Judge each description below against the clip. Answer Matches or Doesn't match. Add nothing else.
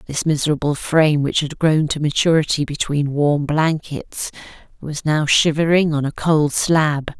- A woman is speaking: Matches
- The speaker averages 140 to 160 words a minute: Matches